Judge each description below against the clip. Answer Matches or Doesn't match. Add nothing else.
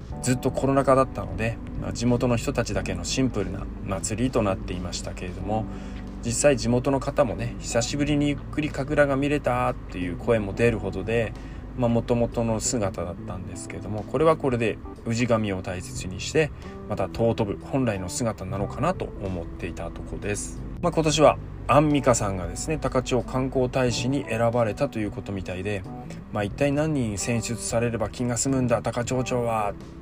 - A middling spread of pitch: Matches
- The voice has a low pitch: Matches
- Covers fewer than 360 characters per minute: Doesn't match